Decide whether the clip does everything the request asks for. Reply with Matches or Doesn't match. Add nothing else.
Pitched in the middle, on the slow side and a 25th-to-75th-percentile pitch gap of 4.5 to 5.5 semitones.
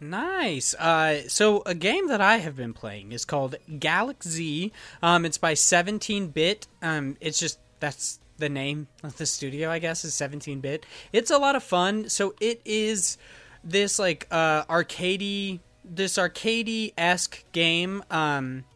Doesn't match